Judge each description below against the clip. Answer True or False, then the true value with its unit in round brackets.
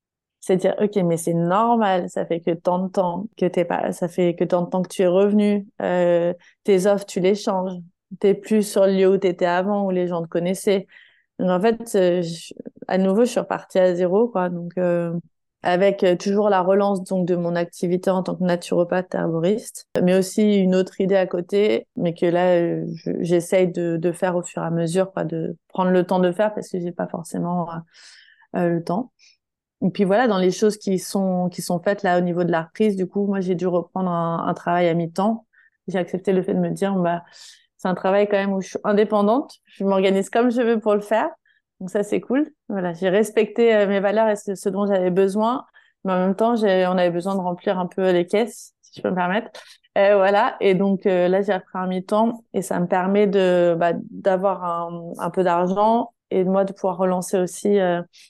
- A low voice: False (190 Hz)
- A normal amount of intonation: False (2.3 semitones)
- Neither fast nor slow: False (240 wpm)